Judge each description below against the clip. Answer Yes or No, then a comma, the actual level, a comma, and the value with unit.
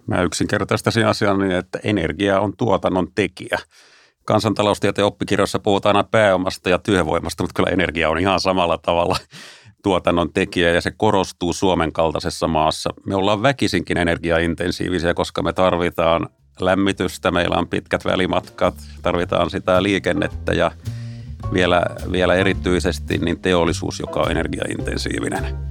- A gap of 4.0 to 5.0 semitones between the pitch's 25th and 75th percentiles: No, average, 2.9 semitones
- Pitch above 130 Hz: No, very low, 90 Hz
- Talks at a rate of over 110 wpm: Yes, average, 130 wpm